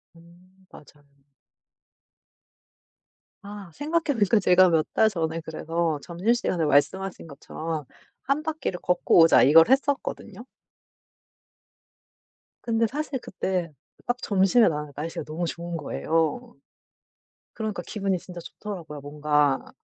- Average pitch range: Yes, average, 5.0 semitones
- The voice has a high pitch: No, medium, 175 Hz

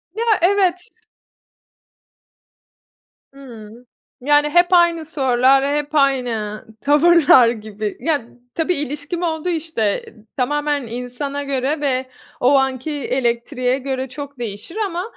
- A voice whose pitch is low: No, very high, 280 Hz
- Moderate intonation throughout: Yes, average, 4.0 semitones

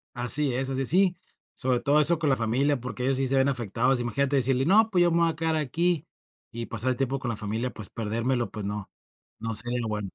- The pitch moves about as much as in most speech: Yes, average, 3.9 semitones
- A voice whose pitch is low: Yes, low, 130 Hz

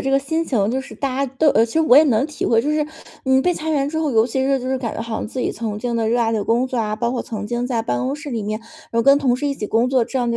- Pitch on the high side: Yes, very high, 250 Hz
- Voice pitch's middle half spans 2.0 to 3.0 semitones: No, average, 3.4 semitones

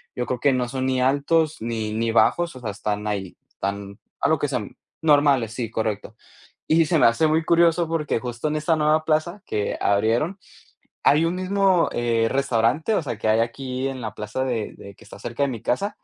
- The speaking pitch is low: Yes, low, 130 Hz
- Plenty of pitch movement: Yes, wide, 5.7 semitones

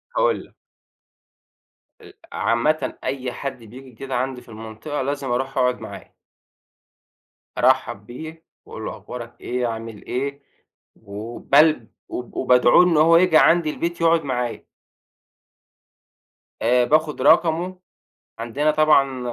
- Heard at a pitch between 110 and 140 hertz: Yes, low, 135 Hz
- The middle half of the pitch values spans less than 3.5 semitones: No, average, 4.3 semitones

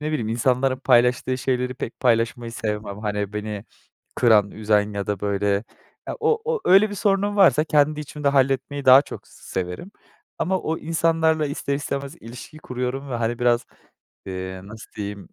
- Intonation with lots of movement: Yes, wide, 5.8 semitones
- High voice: No, low, 125 Hz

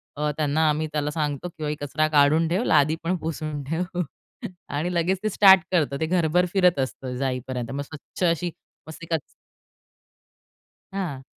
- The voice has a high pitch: No, medium, 155 Hz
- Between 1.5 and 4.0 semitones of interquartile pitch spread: Yes, average, 3.1 semitones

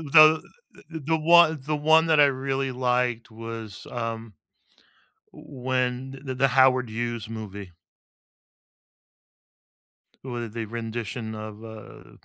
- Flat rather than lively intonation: No, average, 3.2 semitones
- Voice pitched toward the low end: Yes, low, 125 Hz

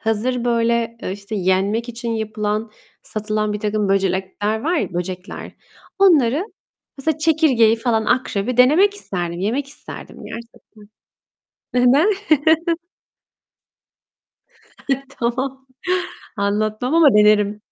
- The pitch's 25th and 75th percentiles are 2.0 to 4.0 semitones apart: Yes, average, 3.6 semitones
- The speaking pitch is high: Yes, high, 225 Hz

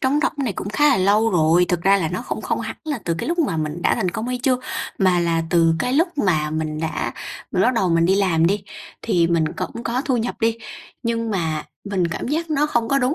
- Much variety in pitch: Yes, wide, 6.9 semitones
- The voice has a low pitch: No, high, 200 Hz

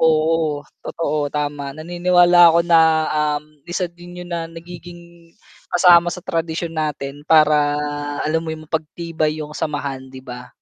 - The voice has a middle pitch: Yes, medium, 160 Hz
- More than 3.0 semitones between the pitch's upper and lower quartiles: No, narrow, 2.5 semitones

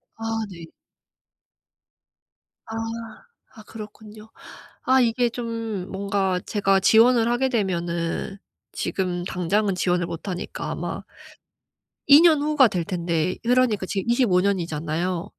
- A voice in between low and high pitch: No, high, 200 Hz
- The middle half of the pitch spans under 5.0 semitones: Yes, average, 4.2 semitones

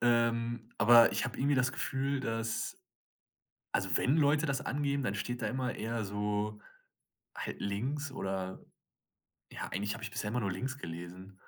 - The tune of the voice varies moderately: Yes, average, 4.4 semitones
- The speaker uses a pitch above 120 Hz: No, low, 115 Hz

